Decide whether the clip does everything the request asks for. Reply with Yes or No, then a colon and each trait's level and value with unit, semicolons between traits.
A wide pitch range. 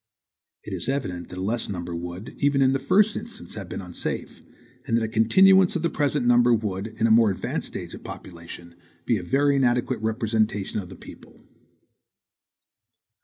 Yes: wide, 6.1 semitones